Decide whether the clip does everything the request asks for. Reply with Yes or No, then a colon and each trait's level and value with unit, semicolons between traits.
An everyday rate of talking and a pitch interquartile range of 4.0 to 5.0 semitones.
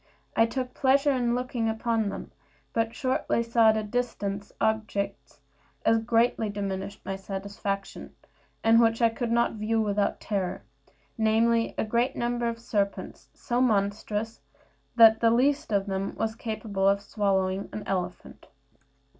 No: average, 145 wpm; narrow, 2.6 semitones